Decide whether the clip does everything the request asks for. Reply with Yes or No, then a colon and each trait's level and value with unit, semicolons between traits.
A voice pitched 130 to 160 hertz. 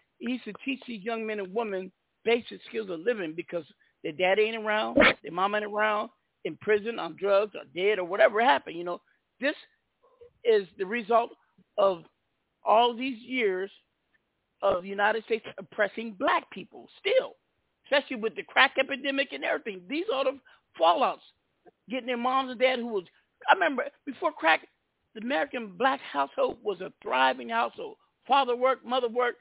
No: high, 235 Hz